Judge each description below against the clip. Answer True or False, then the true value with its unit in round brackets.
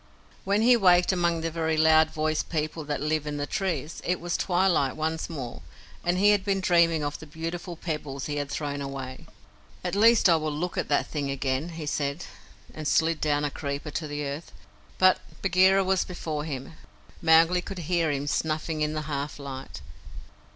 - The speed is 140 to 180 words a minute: False (190 wpm)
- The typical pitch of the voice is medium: True (160 Hz)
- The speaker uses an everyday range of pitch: True (3.2 semitones)